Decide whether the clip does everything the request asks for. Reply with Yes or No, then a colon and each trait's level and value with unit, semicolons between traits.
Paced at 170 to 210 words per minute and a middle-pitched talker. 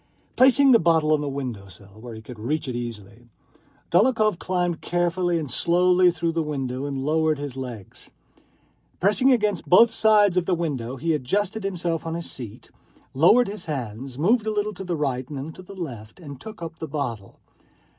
Yes: average, 190 wpm; medium, 160 Hz